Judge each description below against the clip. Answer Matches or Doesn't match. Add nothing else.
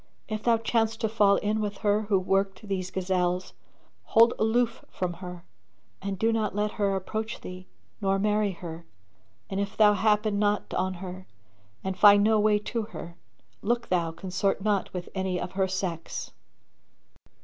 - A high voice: Matches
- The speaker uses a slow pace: Doesn't match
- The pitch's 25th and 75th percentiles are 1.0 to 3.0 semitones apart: Matches